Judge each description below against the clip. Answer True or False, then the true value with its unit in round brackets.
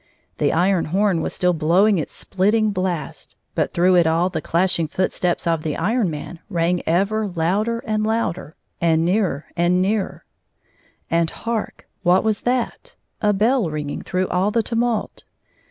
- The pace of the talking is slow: False (165 wpm)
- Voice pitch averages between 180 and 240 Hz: True (185 Hz)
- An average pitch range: True (4.1 semitones)